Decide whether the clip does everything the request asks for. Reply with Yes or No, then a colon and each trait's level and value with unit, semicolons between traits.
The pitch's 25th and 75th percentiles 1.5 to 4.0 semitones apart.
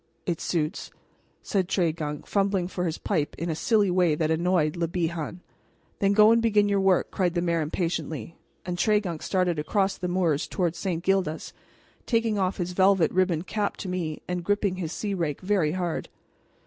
Yes: average, 2.9 semitones